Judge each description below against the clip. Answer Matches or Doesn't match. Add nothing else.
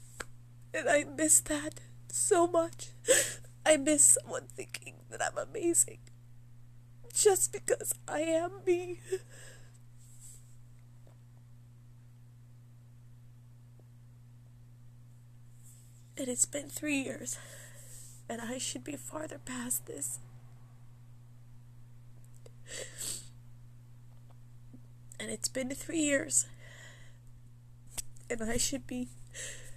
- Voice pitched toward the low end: Matches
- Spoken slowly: Matches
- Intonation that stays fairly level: Matches